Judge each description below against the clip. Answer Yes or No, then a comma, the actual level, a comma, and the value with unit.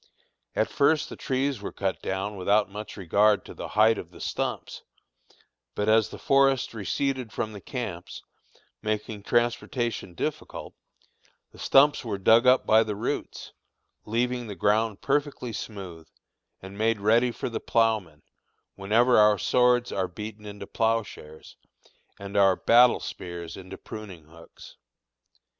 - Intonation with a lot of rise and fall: No, average, 3.4 semitones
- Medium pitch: No, low, 110 Hz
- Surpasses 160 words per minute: No, average, 140 wpm